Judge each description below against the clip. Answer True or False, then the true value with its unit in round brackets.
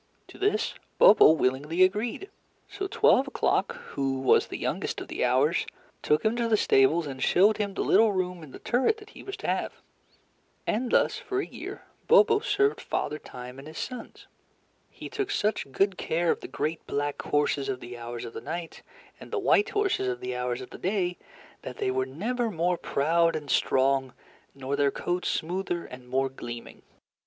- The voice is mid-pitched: True (165 Hz)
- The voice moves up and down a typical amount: False (8.8 semitones)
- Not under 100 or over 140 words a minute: False (190 wpm)